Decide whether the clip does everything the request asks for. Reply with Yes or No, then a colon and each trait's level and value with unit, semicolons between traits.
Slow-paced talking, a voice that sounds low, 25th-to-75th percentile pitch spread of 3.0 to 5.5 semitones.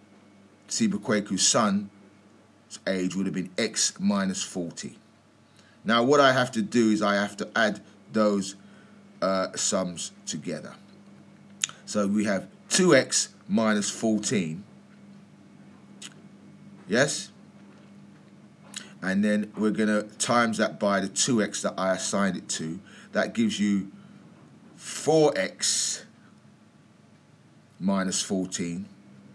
No: slow, 105 wpm; low, 105 Hz; narrow, 2.5 semitones